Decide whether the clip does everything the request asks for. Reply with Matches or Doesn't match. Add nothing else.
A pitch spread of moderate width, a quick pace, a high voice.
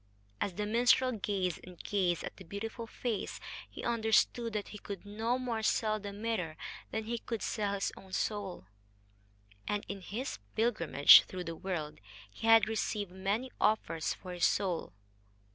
Doesn't match